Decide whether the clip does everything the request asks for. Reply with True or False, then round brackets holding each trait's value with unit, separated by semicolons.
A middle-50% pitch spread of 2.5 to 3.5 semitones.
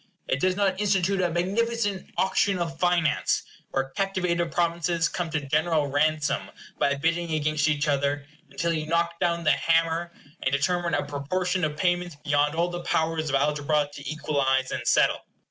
True (3.1 semitones)